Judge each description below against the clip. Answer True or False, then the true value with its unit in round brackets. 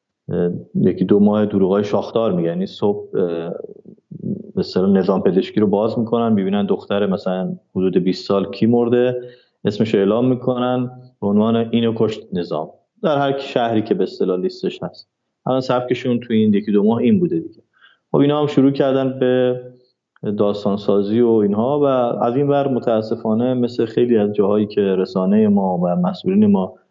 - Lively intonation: False (3.8 semitones)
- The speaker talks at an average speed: False (165 wpm)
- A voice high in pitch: False (115 Hz)